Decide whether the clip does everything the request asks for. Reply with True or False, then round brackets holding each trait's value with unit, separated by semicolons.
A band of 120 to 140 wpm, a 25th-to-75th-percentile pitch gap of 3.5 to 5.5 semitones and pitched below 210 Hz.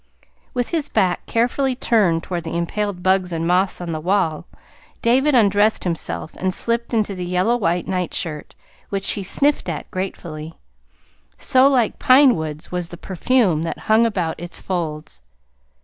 False (155 wpm; 5.2 semitones; 185 Hz)